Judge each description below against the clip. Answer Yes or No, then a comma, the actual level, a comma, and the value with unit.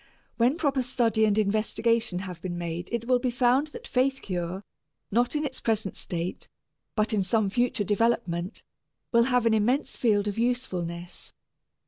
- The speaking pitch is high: Yes, high, 225 Hz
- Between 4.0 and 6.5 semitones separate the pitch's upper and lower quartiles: Yes, average, 4.4 semitones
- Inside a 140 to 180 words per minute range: Yes, average, 160 wpm